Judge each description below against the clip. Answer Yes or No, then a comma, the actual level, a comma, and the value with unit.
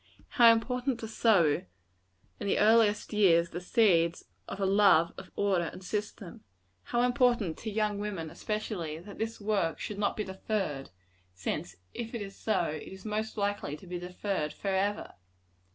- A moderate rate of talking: Yes, average, 165 wpm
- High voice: Yes, high, 205 Hz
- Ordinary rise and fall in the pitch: Yes, average, 3.6 semitones